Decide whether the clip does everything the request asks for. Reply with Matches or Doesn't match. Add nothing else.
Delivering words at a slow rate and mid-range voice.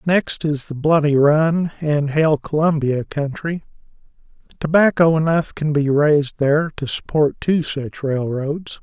Matches